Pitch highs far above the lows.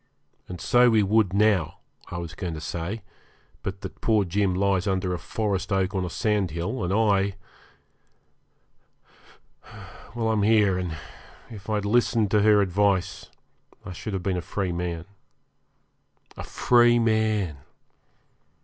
No: average, 2.9 semitones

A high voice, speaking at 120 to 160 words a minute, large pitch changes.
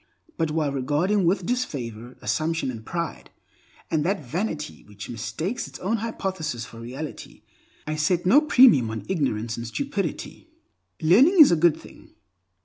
No: medium, 160 Hz; average, 145 wpm; wide, 7.5 semitones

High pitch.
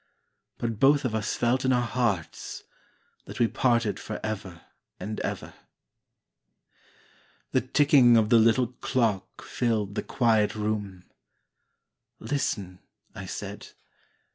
No: low, 115 Hz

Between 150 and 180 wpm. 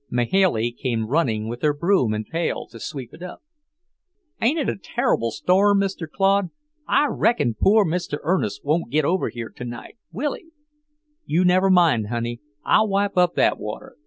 Yes: average, 165 wpm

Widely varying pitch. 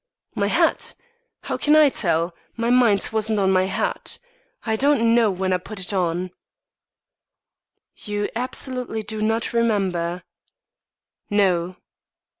No: average, 3.9 semitones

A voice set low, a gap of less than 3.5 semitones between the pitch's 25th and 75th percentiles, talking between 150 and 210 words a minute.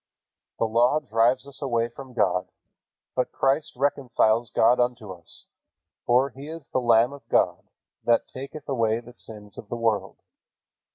Yes: low, 120 Hz; average, 3.1 semitones; average, 155 wpm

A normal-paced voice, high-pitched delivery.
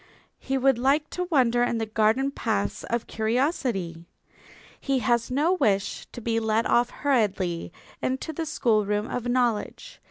Yes: average, 150 wpm; high, 240 Hz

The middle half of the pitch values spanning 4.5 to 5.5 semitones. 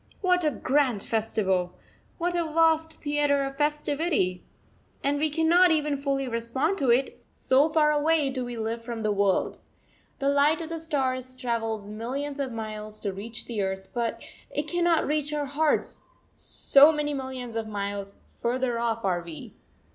Yes: average, 5.0 semitones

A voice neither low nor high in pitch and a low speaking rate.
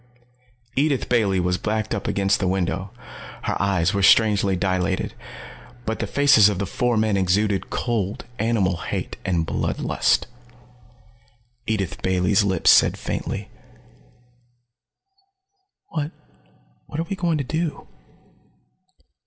No: low, 100 Hz; slow, 120 wpm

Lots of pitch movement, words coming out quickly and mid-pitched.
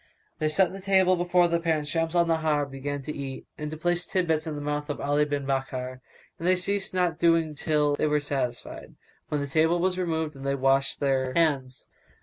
No: average, 3.3 semitones; fast, 225 wpm; medium, 155 Hz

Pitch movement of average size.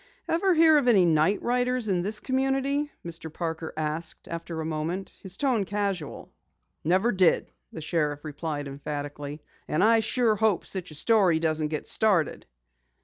No: wide, 6.2 semitones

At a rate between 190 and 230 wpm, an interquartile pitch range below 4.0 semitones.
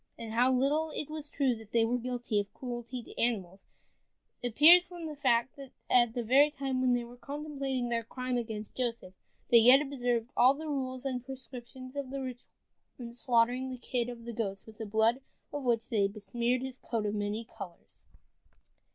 Yes: average, 195 wpm; narrow, 2.5 semitones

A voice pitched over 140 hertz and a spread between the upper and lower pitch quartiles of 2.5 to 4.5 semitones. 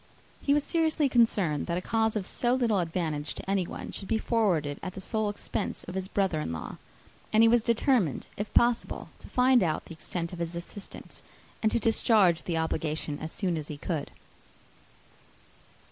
No: high, 190 Hz; wide, 5.6 semitones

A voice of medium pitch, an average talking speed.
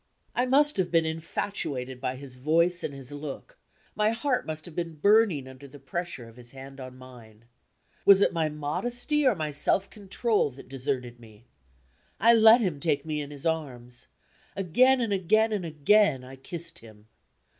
Yes: medium, 155 Hz; average, 175 wpm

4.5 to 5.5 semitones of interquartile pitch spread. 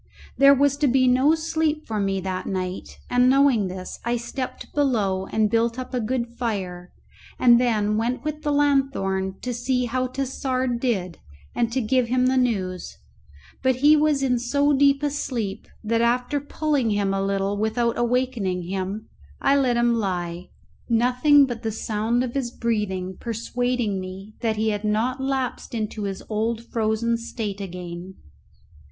No: average, 4.1 semitones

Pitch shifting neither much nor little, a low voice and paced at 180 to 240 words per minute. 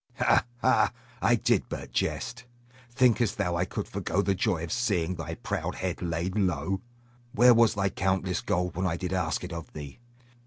Yes: average, 4.1 semitones; very low, 95 Hz; average, 185 wpm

